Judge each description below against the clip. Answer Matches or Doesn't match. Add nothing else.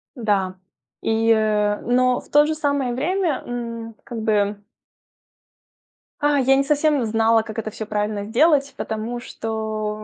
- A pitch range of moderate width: Matches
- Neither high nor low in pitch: Doesn't match